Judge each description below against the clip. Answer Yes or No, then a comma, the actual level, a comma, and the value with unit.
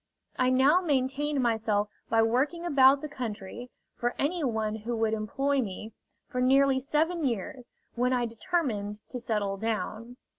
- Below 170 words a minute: Yes, average, 150 wpm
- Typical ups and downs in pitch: Yes, average, 3.9 semitones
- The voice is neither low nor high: No, very high, 250 Hz